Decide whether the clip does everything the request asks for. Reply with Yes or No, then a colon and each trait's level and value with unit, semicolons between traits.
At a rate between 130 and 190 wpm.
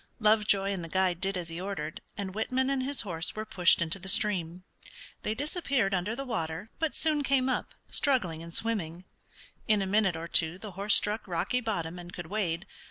No: average, 200 wpm